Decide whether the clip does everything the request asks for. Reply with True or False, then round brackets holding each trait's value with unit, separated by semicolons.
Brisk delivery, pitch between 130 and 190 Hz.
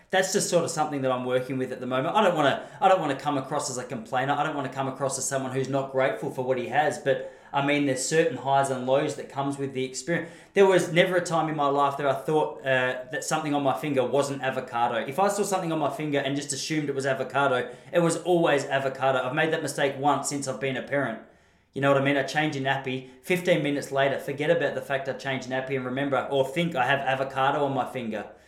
True (270 wpm; 140 Hz)